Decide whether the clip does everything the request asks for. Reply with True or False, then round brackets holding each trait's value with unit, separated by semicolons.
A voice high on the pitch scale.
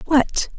True (290 Hz)